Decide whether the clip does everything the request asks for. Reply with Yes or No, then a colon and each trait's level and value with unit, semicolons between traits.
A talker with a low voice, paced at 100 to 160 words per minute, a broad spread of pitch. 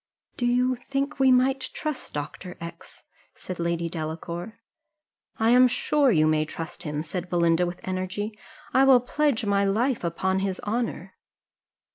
No: high, 195 Hz; average, 155 wpm; wide, 6.7 semitones